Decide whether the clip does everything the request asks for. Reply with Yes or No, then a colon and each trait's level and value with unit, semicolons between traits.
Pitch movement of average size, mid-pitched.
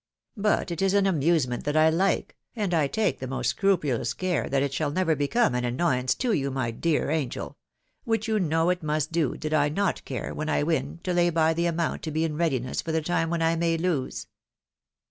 Yes: average, 3.6 semitones; medium, 160 Hz